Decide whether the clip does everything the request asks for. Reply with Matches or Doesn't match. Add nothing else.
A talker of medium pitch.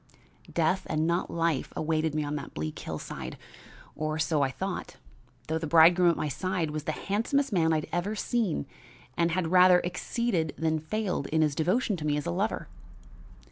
Matches